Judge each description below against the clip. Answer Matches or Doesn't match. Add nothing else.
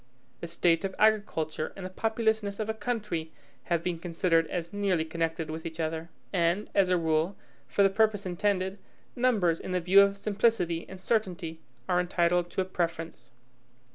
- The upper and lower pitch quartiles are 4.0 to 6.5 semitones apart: Doesn't match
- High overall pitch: Doesn't match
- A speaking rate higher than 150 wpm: Matches